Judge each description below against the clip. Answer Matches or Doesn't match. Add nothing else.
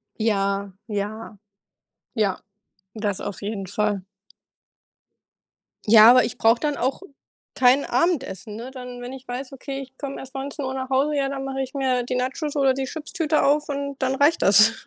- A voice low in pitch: Doesn't match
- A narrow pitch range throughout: Doesn't match